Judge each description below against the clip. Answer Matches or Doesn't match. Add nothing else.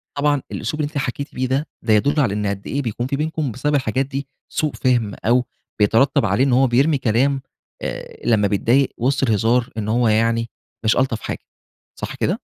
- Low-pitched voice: Matches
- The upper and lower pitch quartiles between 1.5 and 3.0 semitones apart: Doesn't match